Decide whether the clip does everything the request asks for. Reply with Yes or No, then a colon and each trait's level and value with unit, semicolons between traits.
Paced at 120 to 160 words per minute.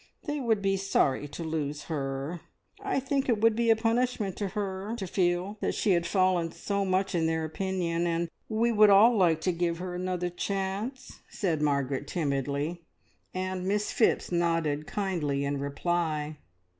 No: average, 170 wpm